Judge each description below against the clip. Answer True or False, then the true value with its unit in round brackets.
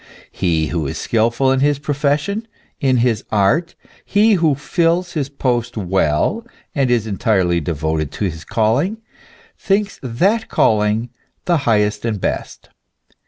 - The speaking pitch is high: False (120 Hz)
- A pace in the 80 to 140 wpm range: True (135 wpm)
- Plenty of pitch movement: True (6.7 semitones)